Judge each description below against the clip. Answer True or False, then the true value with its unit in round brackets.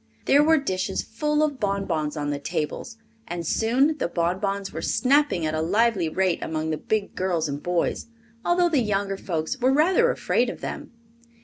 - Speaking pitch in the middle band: False (195 Hz)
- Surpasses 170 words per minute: True (180 wpm)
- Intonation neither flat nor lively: False (8.3 semitones)